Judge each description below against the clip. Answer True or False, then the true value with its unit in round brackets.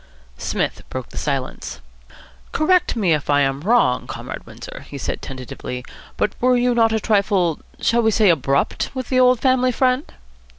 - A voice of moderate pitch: False (220 Hz)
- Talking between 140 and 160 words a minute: False (170 wpm)